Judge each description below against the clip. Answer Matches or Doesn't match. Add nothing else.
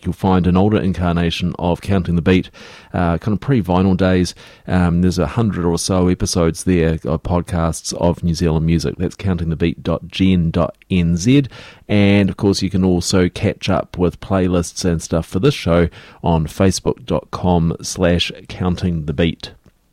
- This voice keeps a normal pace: Matches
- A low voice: Matches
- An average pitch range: Doesn't match